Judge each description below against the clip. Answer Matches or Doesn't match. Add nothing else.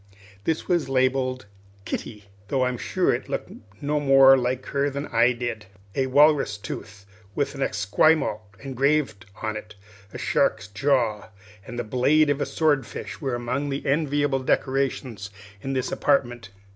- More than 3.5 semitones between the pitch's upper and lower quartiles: Doesn't match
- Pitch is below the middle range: Matches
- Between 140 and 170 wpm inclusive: Matches